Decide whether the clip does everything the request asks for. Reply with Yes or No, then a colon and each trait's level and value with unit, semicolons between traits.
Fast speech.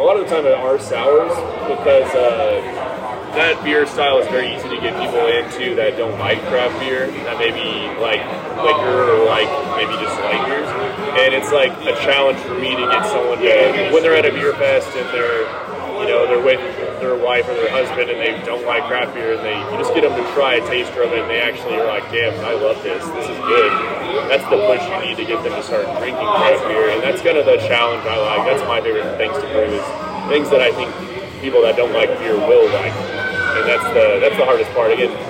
Yes: fast, 240 wpm